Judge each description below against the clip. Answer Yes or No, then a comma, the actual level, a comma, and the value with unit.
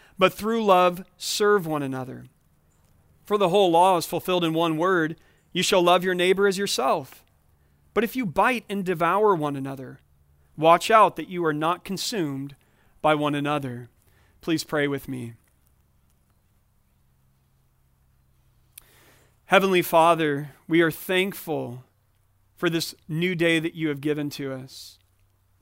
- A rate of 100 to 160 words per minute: Yes, average, 140 wpm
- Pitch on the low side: No, medium, 155 Hz